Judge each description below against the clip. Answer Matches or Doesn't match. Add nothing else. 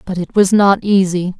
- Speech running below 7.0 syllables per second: Matches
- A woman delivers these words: Matches